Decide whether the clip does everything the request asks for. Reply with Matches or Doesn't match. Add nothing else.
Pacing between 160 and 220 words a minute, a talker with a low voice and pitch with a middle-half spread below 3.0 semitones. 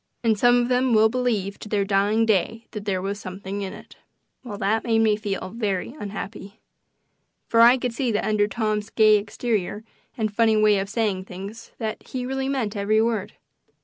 Doesn't match